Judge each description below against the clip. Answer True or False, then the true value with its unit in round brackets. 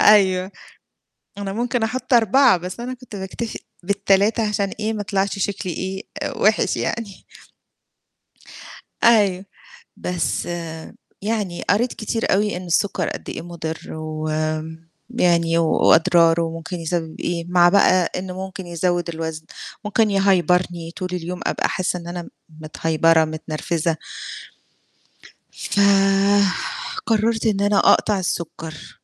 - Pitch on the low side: False (185 Hz)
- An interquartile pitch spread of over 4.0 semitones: False (3.7 semitones)